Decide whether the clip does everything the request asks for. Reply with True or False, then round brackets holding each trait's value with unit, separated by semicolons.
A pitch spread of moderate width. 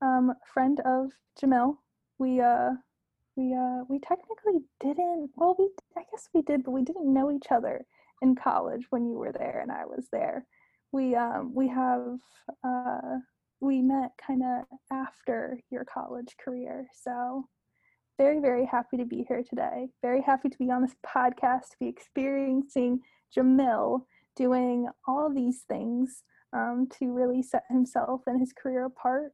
False (1.5 semitones)